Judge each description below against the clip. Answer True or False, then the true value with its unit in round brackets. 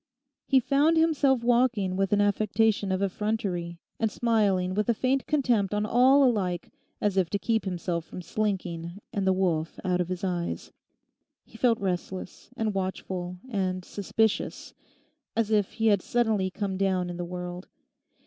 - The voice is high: True (200 Hz)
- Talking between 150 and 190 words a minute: True (160 wpm)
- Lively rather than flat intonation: False (3.5 semitones)